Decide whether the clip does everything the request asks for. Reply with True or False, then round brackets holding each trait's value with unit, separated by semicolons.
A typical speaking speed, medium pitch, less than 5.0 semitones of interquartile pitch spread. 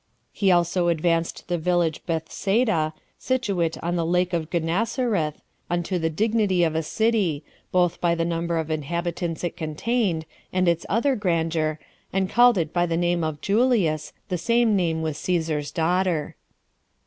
True (155 wpm; 175 Hz; 2.8 semitones)